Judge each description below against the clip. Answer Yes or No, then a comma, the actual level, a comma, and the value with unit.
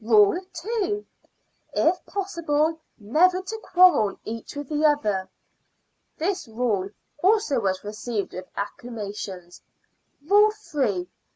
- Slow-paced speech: Yes, slow, 105 wpm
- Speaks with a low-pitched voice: No, very high, 290 Hz